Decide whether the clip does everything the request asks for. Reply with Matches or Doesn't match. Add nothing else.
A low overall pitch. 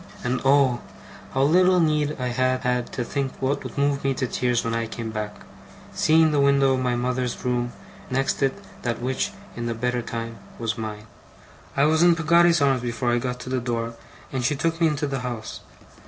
Matches